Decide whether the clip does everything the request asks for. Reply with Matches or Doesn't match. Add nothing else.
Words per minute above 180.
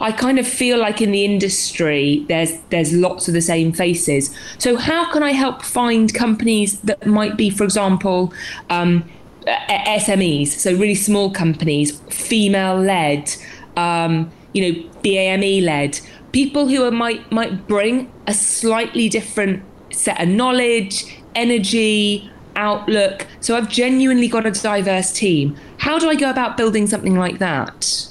Doesn't match